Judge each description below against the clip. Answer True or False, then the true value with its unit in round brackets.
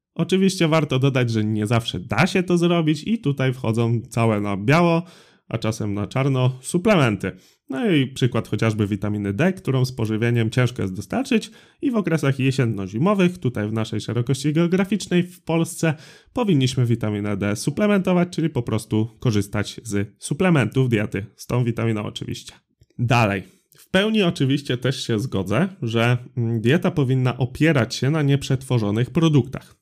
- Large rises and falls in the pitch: True (6.9 semitones)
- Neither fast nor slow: True (150 wpm)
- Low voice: True (130 Hz)